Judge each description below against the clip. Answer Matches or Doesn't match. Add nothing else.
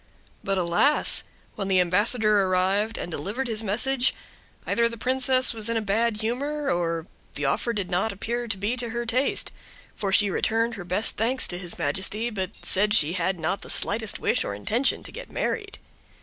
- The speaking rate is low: Doesn't match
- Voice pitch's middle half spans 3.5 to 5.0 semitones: Matches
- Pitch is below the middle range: Doesn't match